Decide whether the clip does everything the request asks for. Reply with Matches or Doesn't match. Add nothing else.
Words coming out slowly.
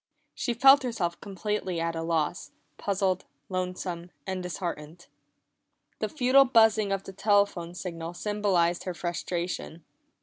Matches